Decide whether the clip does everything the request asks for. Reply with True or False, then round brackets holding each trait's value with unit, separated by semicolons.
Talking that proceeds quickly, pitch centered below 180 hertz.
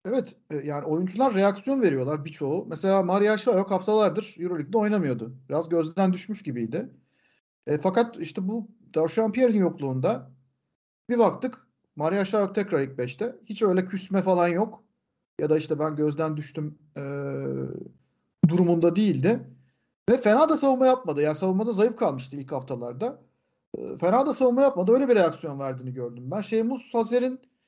False (145 wpm; 185 Hz)